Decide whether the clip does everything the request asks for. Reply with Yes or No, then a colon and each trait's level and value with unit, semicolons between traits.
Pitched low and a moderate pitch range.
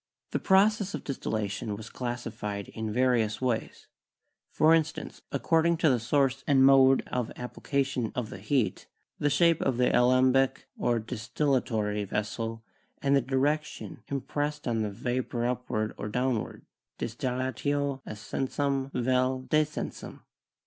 Yes: low, 130 Hz; average, 3.5 semitones